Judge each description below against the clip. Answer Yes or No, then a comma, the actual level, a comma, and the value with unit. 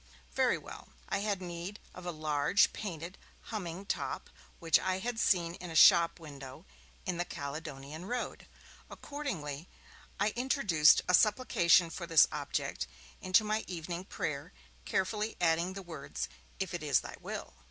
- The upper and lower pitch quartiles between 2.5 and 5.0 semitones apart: Yes, average, 3.8 semitones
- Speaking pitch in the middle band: Yes, medium, 175 Hz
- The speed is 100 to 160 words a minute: Yes, average, 150 wpm